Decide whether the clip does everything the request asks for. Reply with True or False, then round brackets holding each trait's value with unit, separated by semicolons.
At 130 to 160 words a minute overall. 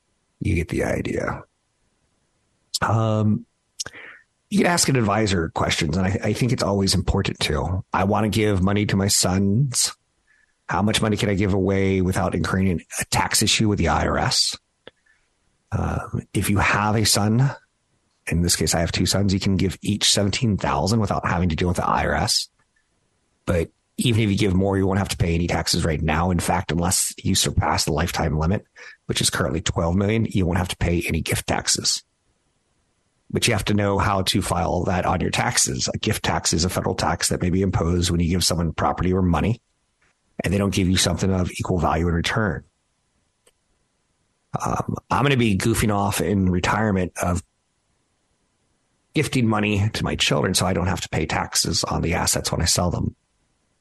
False (195 wpm)